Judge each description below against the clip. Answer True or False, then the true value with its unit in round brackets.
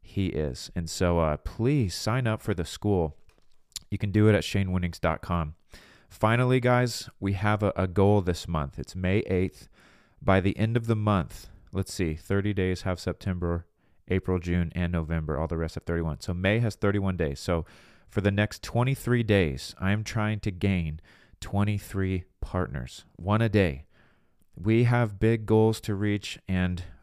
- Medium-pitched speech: False (95 Hz)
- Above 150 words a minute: True (170 wpm)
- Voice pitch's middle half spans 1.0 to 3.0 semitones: False (3.6 semitones)